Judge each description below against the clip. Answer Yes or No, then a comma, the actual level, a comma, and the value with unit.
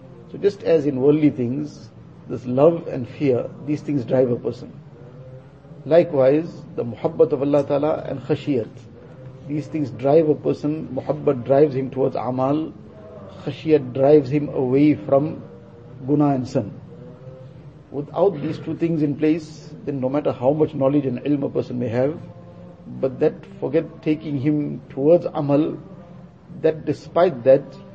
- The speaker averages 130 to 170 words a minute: Yes, average, 150 wpm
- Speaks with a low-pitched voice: No, medium, 145 Hz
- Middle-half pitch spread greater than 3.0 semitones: No, average, 2.7 semitones